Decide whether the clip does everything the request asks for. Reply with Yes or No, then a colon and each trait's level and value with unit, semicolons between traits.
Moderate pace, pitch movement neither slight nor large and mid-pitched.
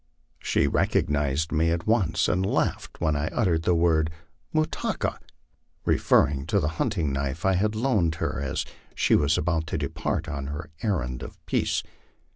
No: average, 170 wpm; average, 4.2 semitones; very low, 80 Hz